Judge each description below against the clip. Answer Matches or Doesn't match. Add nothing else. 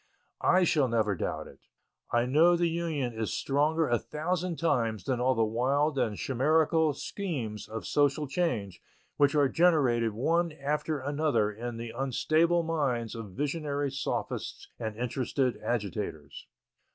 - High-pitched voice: Doesn't match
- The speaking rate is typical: Matches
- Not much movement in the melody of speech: Doesn't match